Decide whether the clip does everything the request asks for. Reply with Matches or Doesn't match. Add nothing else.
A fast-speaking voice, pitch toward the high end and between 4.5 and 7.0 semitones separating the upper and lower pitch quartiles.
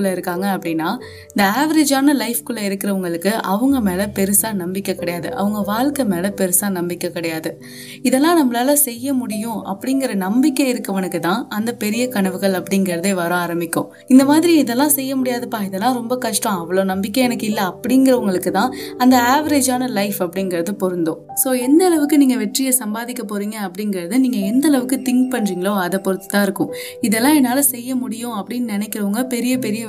Matches